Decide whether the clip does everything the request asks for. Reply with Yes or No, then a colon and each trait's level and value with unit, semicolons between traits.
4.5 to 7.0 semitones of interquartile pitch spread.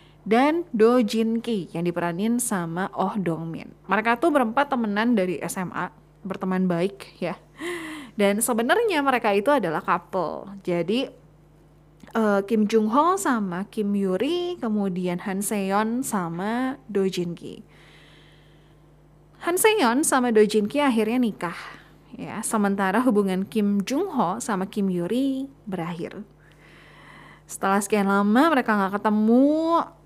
Yes: average, 5.2 semitones